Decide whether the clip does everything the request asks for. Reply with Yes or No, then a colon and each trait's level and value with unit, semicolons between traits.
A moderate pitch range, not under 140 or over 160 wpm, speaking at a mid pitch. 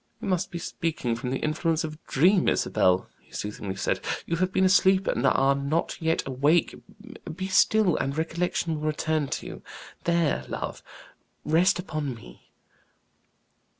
Yes: average, 4.3 semitones; average, 155 wpm; medium, 160 Hz